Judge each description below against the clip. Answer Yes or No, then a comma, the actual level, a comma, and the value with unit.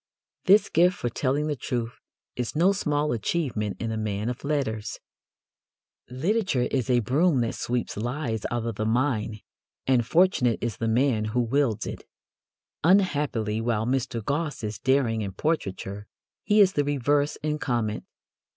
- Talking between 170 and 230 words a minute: No, average, 155 wpm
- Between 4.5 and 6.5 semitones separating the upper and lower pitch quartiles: Yes, average, 4.8 semitones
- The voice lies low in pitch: Yes, low, 125 Hz